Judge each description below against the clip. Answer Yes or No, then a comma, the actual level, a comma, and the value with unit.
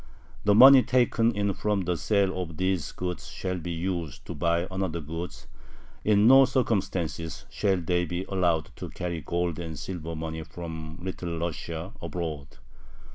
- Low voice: Yes, very low, 90 Hz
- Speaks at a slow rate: No, average, 155 wpm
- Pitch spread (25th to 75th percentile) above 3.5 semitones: No, average, 2.9 semitones